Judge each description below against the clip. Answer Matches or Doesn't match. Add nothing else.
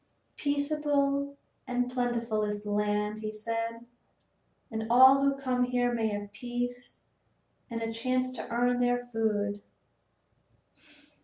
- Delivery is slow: Matches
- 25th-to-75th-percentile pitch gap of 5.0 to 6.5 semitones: Doesn't match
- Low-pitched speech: Doesn't match